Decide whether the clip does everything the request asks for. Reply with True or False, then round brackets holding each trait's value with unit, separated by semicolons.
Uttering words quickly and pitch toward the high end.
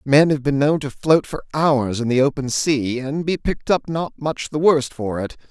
False (220 wpm; 140 Hz)